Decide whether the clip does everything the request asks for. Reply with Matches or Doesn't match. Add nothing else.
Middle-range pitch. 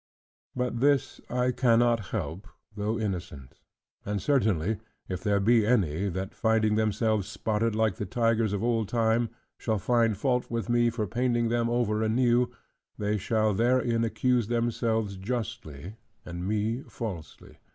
Doesn't match